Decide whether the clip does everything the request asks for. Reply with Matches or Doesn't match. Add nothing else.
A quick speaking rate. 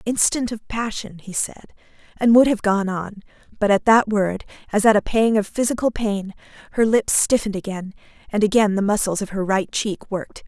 Doesn't match